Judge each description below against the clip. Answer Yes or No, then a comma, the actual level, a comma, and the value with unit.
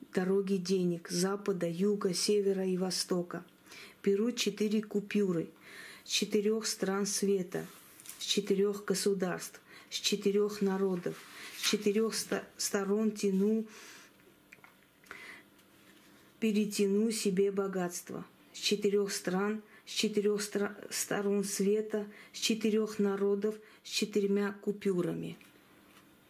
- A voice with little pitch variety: Yes, narrow, 1.3 semitones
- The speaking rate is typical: No, slow, 90 wpm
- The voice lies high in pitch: Yes, high, 205 Hz